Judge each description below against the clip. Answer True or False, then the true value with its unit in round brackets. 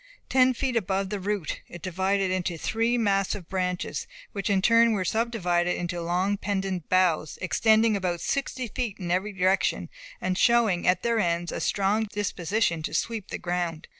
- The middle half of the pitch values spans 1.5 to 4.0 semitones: True (3.6 semitones)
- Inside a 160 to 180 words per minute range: True (165 wpm)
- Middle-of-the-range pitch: False (195 Hz)